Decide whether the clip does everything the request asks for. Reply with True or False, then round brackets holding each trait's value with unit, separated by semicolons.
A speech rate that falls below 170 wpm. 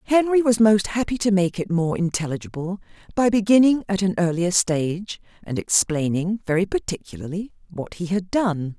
True (155 wpm)